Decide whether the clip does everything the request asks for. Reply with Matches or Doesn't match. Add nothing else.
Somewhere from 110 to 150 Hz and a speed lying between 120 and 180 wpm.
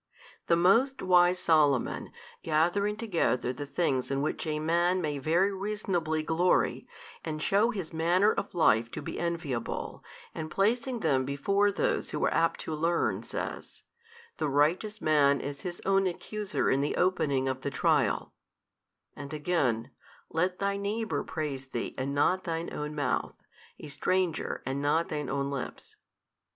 Doesn't match